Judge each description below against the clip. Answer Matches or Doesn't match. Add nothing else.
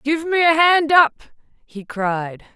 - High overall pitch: Matches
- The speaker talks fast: Doesn't match